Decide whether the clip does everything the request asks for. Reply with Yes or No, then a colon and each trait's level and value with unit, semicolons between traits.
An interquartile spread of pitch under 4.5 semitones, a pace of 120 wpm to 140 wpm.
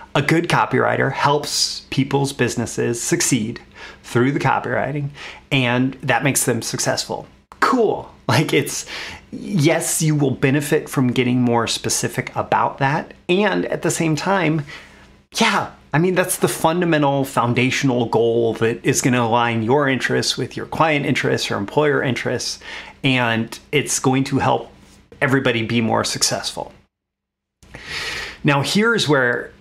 No: average, 4.8 semitones; slow, 135 wpm